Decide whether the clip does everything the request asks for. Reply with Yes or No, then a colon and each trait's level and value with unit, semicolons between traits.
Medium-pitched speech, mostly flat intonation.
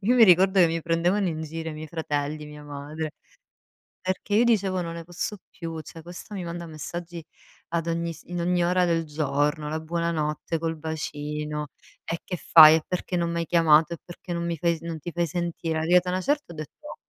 Yes: medium, 165 Hz; narrow, 2.1 semitones